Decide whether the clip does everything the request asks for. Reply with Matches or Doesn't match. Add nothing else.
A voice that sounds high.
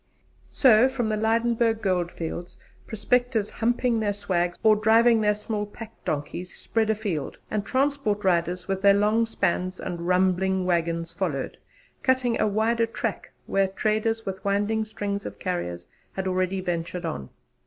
Matches